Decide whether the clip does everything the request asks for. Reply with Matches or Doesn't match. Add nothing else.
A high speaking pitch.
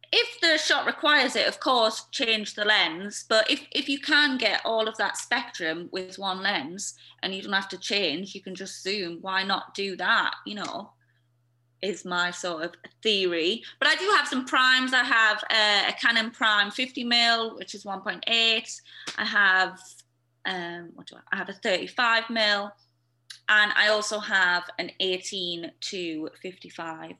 Matches